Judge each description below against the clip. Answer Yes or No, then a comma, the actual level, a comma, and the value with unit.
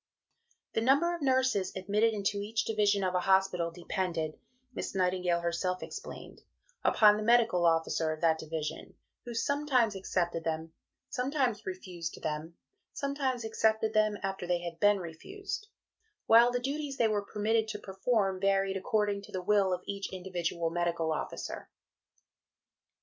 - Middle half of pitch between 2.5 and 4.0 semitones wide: No, average, 4.4 semitones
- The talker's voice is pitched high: Yes, high, 195 Hz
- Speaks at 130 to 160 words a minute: Yes, average, 150 wpm